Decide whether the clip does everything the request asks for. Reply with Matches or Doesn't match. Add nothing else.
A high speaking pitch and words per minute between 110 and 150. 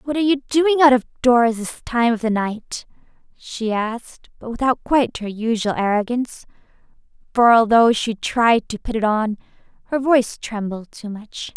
Doesn't match